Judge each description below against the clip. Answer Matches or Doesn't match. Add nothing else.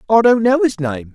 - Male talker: Matches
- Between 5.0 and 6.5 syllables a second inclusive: Matches